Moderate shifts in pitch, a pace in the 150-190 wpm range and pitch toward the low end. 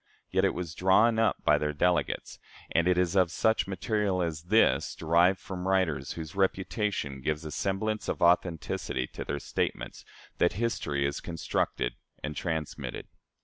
Yes: average, 3.7 semitones; average, 155 wpm; very low, 90 Hz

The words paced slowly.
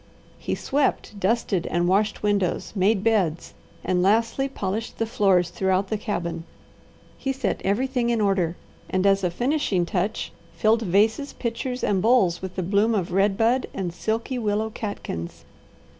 No: average, 155 wpm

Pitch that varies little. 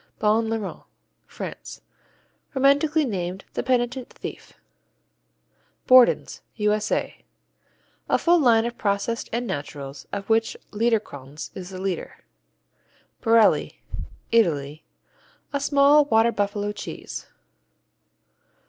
No: average, 3.9 semitones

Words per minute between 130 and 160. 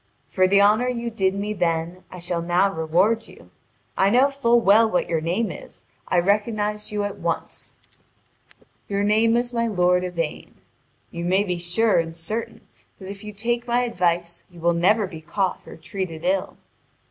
No: average, 180 wpm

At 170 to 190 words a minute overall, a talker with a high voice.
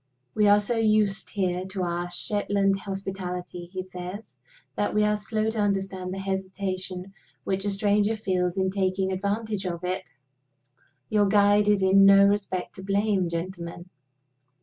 No: average, 150 wpm; high, 195 Hz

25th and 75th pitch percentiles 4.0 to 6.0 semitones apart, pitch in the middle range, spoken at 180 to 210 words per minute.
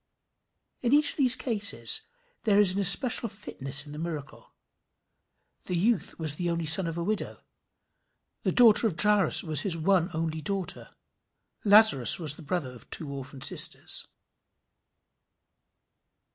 No: average, 5.1 semitones; medium, 175 Hz; average, 145 wpm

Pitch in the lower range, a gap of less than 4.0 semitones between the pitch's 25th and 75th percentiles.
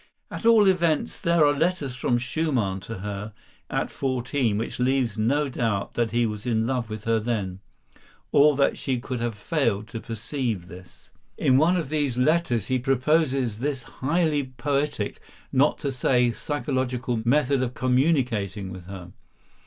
No: low, 125 Hz; average, 4.4 semitones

